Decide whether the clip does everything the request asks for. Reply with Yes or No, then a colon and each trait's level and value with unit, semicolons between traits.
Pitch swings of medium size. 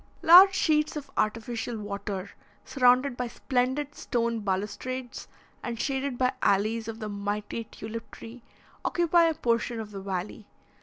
Yes: average, 3.9 semitones